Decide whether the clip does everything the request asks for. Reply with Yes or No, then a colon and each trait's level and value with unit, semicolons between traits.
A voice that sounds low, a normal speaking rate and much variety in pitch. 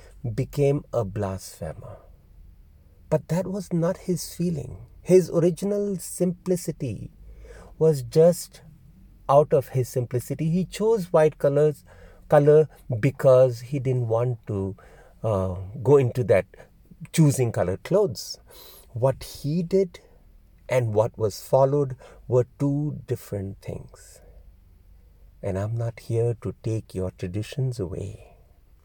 No: low, 125 Hz; slow, 115 wpm; wide, 7.9 semitones